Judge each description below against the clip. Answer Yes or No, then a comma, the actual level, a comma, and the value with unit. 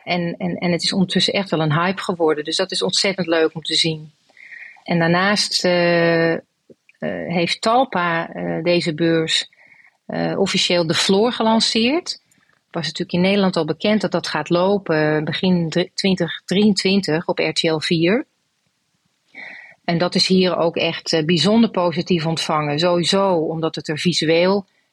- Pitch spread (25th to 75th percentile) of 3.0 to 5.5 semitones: No, narrow, 2.6 semitones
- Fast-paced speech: No, average, 150 wpm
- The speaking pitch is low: No, medium, 175 Hz